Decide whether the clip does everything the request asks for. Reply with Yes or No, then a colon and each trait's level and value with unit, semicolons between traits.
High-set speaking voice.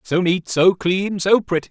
No: medium, 180 Hz